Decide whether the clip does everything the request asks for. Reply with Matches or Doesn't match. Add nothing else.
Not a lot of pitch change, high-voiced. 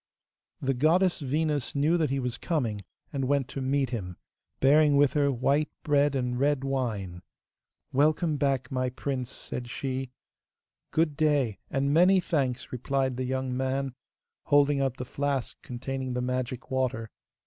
Doesn't match